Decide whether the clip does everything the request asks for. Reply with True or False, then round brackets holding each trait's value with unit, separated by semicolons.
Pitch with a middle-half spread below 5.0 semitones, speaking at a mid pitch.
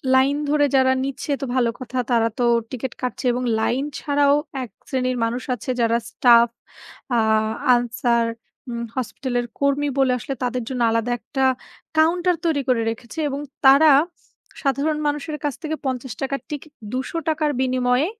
False (2.9 semitones; 260 Hz)